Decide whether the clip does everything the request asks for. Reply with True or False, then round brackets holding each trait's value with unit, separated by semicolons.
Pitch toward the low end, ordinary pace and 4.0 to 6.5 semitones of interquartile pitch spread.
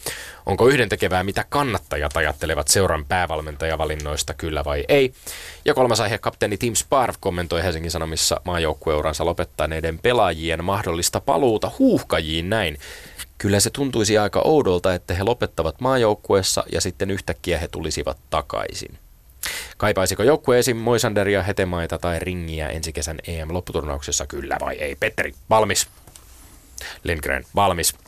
True (90 Hz; 125 wpm; 4.7 semitones)